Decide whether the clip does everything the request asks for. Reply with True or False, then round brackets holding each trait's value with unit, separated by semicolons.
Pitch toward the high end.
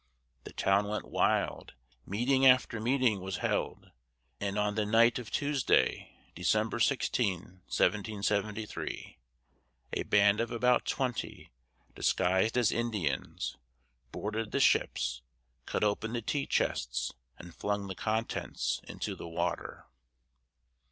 False (105 Hz)